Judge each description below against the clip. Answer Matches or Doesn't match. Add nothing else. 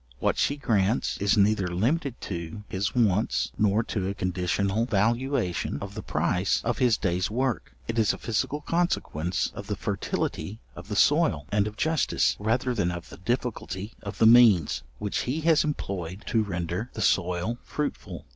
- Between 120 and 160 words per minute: Doesn't match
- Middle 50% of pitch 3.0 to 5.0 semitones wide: Matches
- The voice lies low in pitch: Matches